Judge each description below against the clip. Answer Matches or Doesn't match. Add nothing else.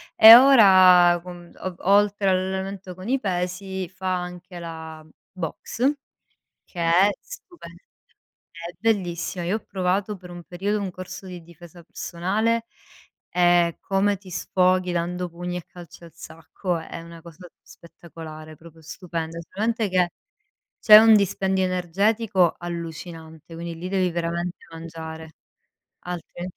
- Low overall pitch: Doesn't match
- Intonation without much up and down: Matches